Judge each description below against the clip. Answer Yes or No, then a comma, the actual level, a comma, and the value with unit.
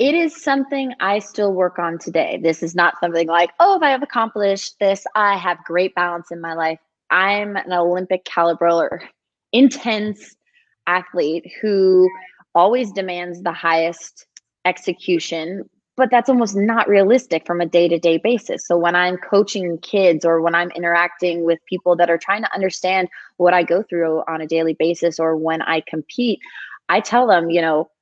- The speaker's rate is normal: Yes, average, 180 wpm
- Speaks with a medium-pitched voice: Yes, medium, 180 Hz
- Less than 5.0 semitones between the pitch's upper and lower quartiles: Yes, average, 3.2 semitones